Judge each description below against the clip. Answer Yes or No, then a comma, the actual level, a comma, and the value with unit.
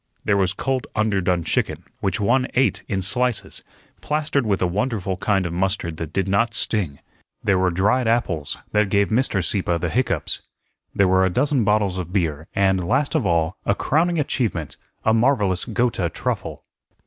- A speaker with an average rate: Yes, average, 170 wpm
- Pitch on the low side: Yes, low, 100 Hz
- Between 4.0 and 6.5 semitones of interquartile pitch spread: Yes, average, 4.5 semitones